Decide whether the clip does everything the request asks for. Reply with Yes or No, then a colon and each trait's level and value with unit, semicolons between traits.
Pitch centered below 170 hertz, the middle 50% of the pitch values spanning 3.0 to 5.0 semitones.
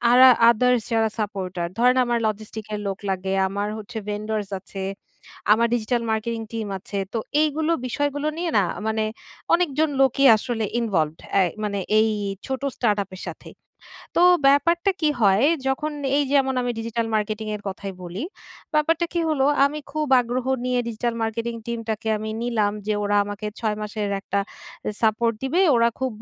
No: high, 225 Hz; average, 3.8 semitones